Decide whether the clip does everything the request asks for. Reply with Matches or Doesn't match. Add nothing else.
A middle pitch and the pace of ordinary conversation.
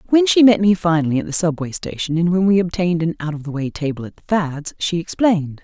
Doesn't match